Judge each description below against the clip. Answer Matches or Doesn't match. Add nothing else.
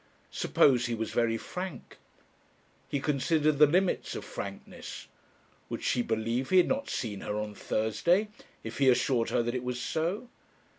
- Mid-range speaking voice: Doesn't match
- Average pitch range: Doesn't match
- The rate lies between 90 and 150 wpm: Doesn't match